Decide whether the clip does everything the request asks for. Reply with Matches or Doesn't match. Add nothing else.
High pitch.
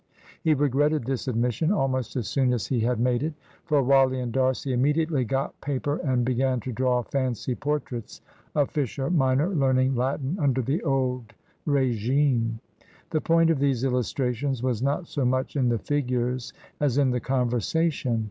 Doesn't match